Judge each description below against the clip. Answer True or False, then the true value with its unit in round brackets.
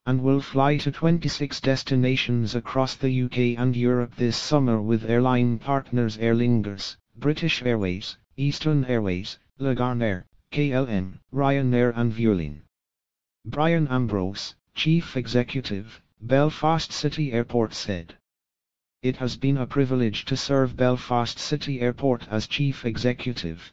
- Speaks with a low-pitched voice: True (125 Hz)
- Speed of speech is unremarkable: False (125 wpm)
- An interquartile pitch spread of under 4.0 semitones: True (3.6 semitones)